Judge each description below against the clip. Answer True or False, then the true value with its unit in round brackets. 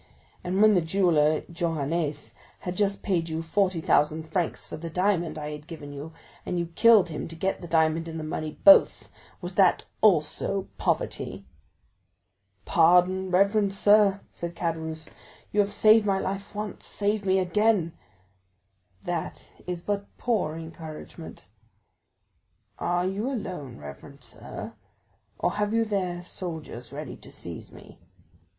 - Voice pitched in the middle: True (175 Hz)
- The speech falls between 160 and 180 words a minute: False (140 wpm)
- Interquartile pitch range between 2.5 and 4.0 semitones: True (3.7 semitones)